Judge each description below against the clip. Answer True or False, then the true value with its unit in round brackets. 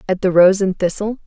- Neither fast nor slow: False (240 wpm)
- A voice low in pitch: False (190 Hz)